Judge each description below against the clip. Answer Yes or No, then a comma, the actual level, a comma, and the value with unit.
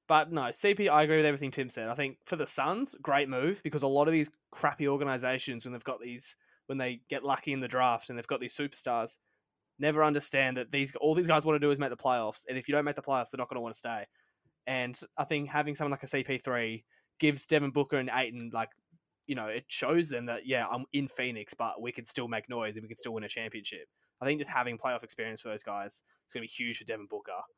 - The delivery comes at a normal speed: No, fast, 265 wpm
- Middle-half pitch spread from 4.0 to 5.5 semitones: No, average, 3.4 semitones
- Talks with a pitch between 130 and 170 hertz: Yes, low, 135 Hz